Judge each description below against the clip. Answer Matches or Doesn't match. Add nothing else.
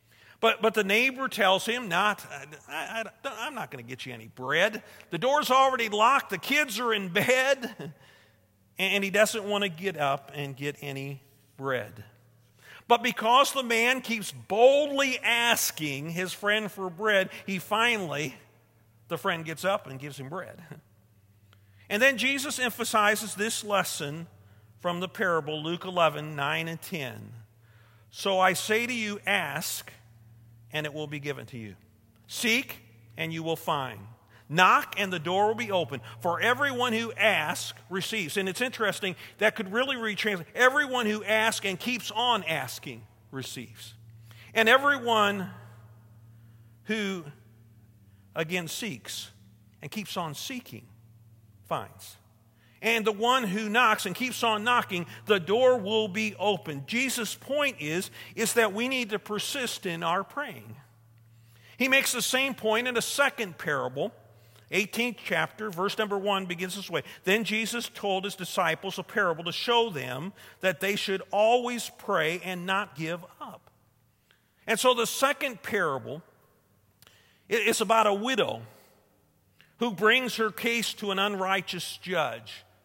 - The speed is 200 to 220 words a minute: Doesn't match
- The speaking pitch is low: Doesn't match